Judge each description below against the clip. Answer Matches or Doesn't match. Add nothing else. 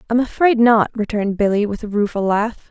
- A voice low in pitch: Doesn't match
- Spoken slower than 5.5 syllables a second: Doesn't match